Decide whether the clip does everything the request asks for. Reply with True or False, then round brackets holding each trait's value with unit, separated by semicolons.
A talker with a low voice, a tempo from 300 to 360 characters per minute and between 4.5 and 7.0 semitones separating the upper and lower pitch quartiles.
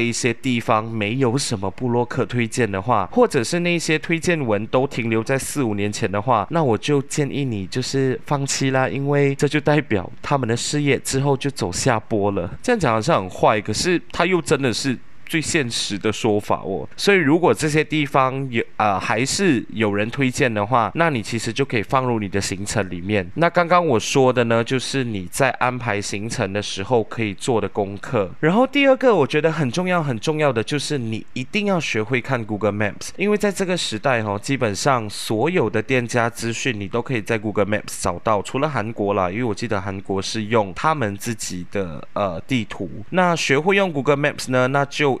True (125 Hz; 330 characters per minute; 5.1 semitones)